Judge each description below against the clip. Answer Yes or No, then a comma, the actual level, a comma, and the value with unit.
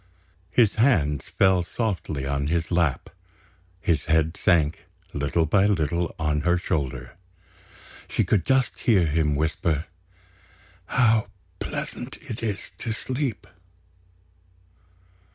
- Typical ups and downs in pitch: No, wide, 5.9 semitones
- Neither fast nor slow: No, slow, 110 wpm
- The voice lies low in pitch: Yes, very low, 85 Hz